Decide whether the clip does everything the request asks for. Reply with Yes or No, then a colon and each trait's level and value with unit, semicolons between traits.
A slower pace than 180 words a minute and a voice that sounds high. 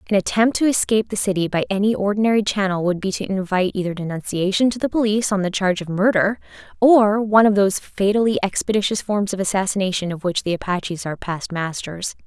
No: average, 195 wpm; high, 200 Hz